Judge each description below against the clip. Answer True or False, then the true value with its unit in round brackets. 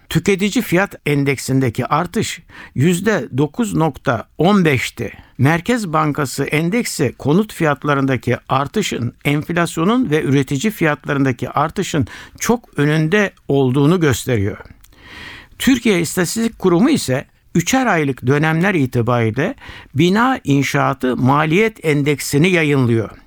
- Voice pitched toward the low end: False (150 Hz)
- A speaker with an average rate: False (85 wpm)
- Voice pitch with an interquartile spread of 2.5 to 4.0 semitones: False (5.4 semitones)